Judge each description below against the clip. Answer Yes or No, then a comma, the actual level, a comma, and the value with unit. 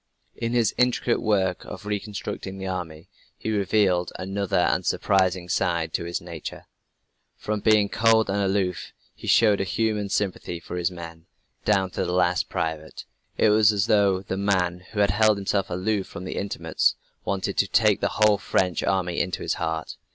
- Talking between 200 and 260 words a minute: No, average, 175 wpm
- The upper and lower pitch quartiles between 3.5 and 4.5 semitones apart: No, average, 2.8 semitones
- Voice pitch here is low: Yes, very low, 95 Hz